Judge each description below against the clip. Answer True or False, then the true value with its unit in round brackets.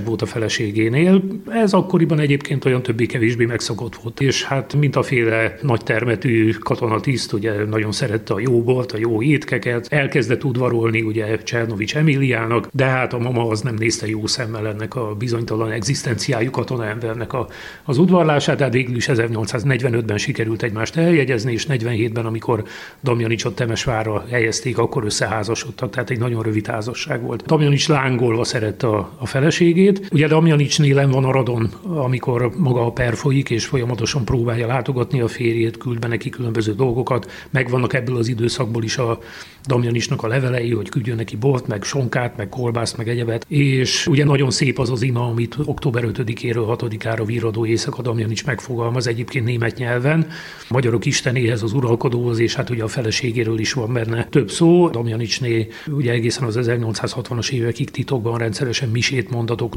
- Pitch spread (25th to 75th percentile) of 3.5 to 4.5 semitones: False (2.8 semitones)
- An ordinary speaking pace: False (160 wpm)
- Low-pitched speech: True (120 Hz)